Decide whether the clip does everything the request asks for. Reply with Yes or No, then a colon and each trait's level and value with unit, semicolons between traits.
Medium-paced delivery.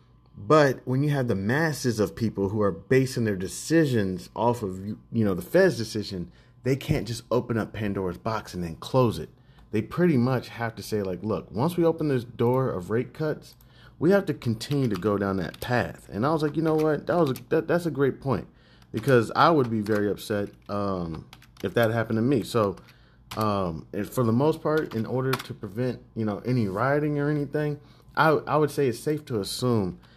No: fast, 215 wpm